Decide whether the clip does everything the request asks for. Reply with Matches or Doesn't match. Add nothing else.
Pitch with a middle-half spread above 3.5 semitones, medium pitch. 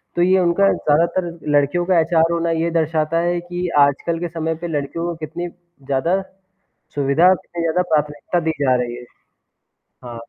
Doesn't match